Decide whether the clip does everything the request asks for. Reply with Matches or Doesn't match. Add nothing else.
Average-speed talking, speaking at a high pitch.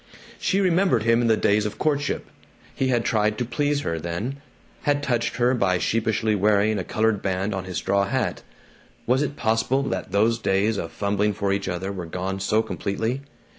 Doesn't match